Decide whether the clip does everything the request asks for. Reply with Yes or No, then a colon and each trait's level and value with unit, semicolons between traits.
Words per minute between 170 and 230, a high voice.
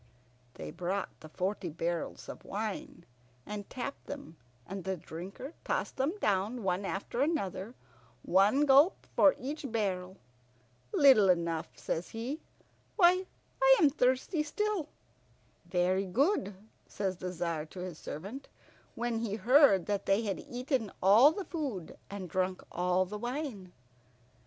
No: slow, 135 wpm; high, 210 Hz